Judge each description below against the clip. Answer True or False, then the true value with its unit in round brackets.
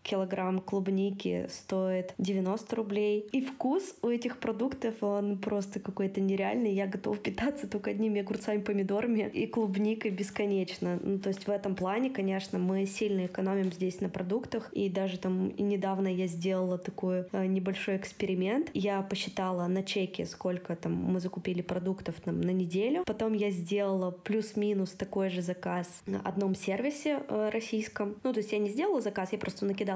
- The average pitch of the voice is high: True (195 Hz)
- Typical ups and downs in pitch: False (2.2 semitones)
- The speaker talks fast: True (165 wpm)